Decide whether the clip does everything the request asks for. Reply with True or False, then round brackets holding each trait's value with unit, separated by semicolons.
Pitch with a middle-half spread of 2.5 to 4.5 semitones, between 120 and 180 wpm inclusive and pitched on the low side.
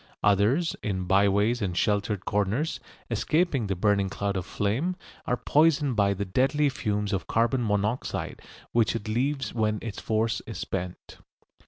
True (3.8 semitones; 150 wpm; 105 Hz)